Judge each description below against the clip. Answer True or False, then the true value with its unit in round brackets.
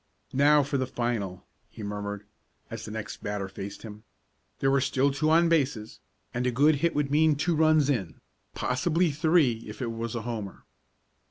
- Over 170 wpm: True (180 wpm)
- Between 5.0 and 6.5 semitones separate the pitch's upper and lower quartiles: True (5.6 semitones)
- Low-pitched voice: True (130 Hz)